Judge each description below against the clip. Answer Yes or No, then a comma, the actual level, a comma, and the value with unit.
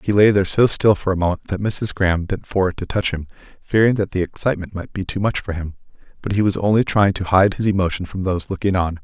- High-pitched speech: No, very low, 95 Hz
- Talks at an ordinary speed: No, fast, 260 wpm